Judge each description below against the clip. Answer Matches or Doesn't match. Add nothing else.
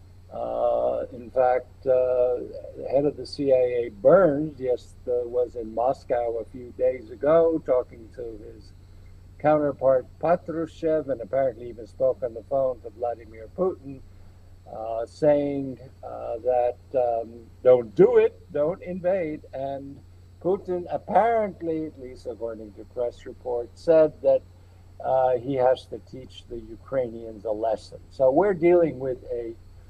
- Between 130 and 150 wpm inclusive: Matches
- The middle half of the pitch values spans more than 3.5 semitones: Matches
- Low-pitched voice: Matches